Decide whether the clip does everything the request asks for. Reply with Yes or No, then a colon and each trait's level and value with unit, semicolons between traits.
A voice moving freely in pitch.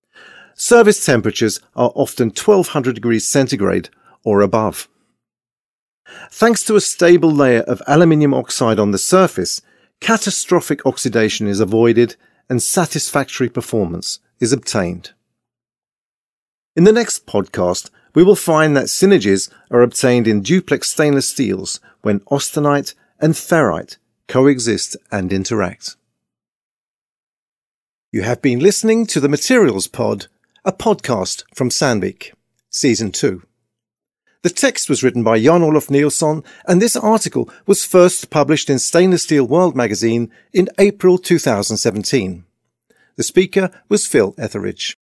Yes: wide, 7.6 semitones